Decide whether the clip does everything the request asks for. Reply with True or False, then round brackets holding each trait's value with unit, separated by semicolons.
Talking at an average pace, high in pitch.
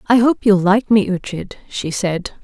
True (195 wpm; 200 Hz)